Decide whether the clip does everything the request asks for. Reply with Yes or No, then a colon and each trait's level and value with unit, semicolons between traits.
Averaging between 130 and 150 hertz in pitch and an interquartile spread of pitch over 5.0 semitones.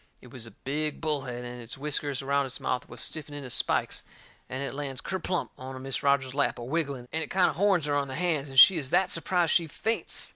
No: medium, 140 Hz; average, 3.3 semitones